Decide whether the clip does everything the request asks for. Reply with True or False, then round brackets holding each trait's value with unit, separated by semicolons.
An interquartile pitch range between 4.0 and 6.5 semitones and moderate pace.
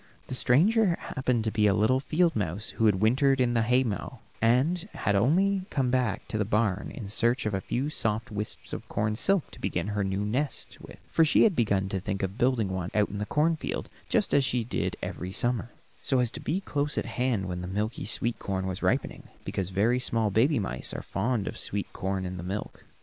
False (4.6 semitones; 225 wpm)